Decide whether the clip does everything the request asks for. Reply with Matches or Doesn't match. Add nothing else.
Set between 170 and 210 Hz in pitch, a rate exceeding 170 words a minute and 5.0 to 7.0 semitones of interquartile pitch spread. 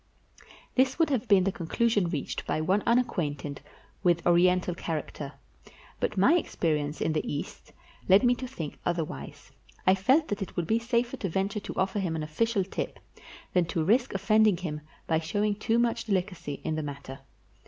Matches